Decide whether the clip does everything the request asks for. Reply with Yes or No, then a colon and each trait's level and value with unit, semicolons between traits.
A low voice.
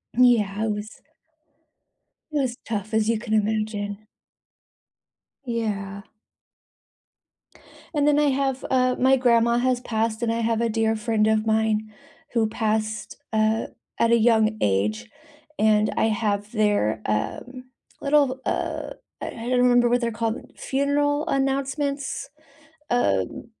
No: high, 225 Hz